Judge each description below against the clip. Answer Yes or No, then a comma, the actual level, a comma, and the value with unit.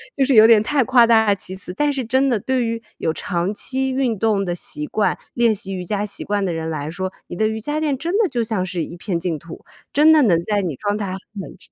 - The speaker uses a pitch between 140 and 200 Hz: No, high, 215 Hz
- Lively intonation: Yes, wide, 5.7 semitones